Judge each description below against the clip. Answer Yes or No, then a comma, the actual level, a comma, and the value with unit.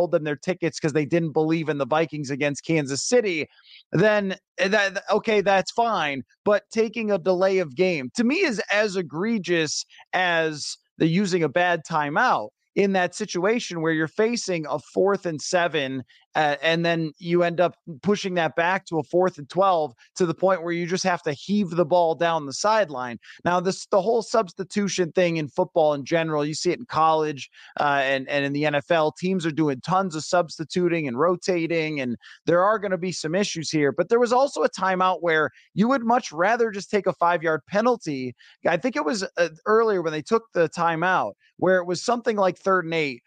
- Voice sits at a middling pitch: Yes, medium, 175 Hz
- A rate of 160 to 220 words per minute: Yes, fast, 205 wpm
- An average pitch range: Yes, average, 3.8 semitones